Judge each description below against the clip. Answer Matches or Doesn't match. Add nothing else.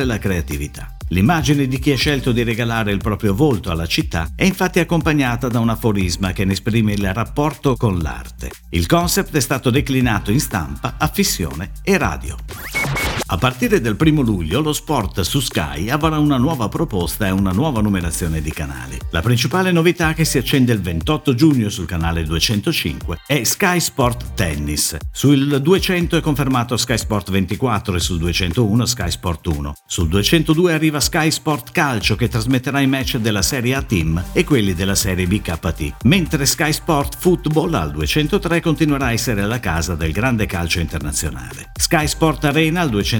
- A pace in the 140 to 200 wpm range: Matches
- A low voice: Matches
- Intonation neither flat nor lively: Doesn't match